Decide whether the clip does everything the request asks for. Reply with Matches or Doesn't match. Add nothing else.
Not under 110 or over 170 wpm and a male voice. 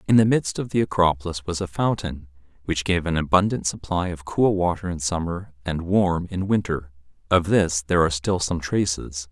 Doesn't match